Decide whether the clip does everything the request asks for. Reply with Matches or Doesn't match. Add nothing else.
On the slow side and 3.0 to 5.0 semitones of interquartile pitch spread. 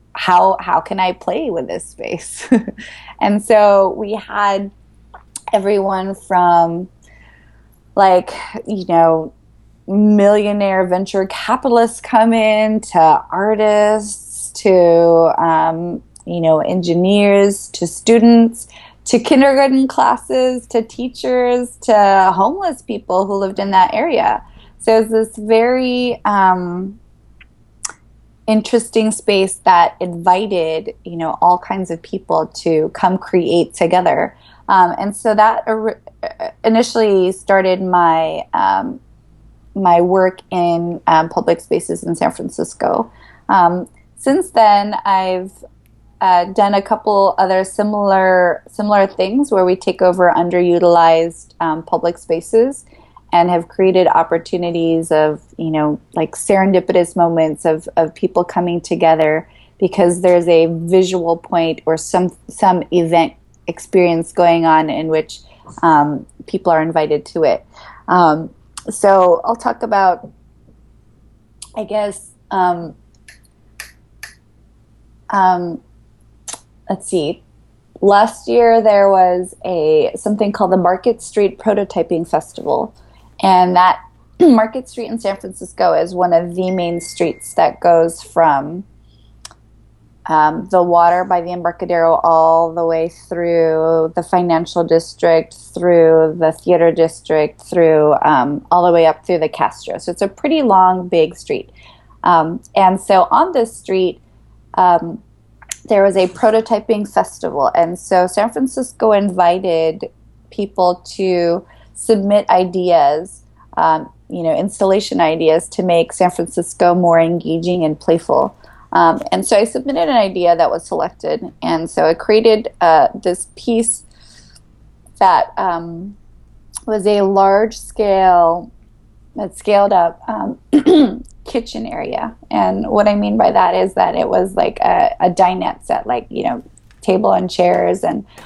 Matches